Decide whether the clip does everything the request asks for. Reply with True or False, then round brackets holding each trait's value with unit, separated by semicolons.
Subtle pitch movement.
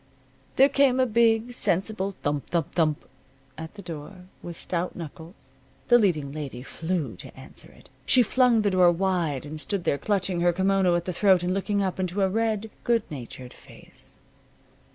False (4.6 semitones)